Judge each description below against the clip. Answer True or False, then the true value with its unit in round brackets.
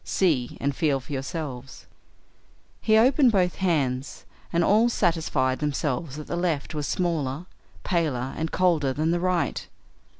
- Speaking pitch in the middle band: True (160 Hz)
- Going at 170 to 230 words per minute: False (140 wpm)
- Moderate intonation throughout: True (4.7 semitones)